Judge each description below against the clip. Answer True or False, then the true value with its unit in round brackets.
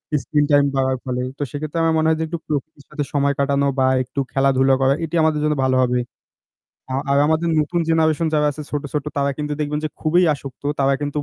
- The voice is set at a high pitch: False (145 Hz)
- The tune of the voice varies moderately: False (2.2 semitones)